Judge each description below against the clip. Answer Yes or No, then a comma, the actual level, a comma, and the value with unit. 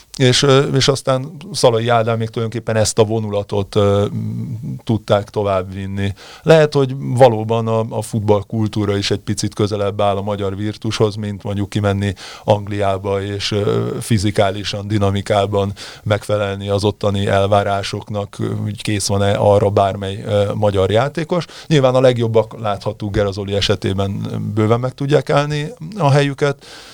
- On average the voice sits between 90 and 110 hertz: Yes, low, 105 Hz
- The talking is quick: No, average, 135 wpm